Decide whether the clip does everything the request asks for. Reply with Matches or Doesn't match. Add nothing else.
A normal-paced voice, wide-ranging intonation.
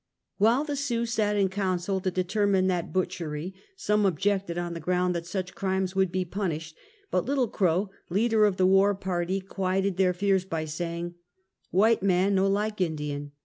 Doesn't match